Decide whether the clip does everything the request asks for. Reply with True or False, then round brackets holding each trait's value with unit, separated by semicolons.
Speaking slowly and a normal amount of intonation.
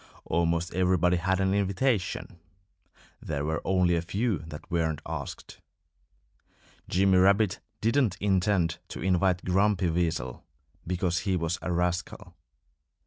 False (120 wpm; 2.2 semitones)